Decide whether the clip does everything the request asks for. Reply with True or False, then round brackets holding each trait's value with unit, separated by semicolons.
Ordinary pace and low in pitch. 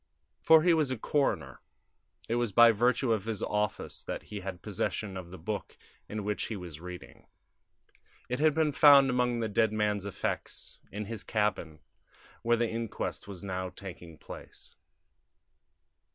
True (160 wpm; 105 Hz)